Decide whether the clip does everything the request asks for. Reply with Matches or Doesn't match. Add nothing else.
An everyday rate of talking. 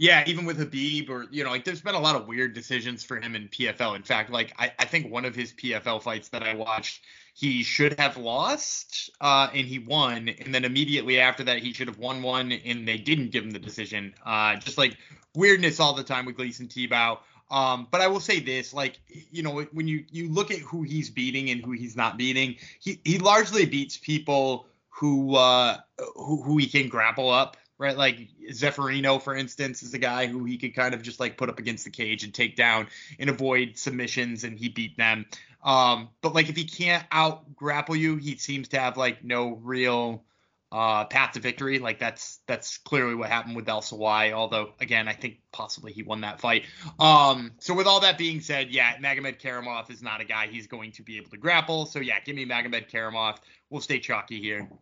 Doesn't match